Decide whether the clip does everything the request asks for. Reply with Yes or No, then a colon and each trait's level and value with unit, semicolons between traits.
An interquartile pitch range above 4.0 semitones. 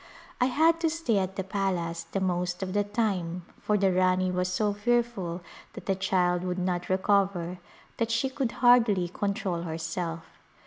No: average, 3.0 semitones